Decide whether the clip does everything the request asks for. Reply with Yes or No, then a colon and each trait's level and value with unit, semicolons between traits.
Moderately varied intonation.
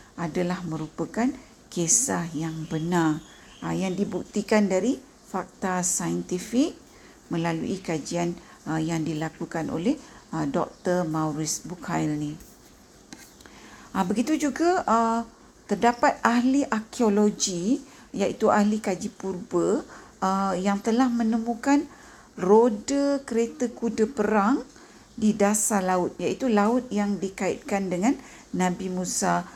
Yes: average, 5.0 semitones